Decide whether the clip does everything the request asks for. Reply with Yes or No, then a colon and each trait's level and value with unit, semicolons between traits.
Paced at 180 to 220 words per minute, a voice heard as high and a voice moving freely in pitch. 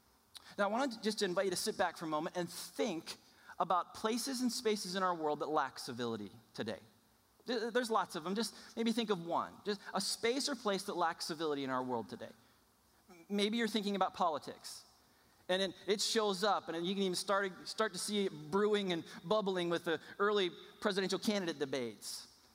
No: average, 195 wpm; high, 195 Hz; average, 4.2 semitones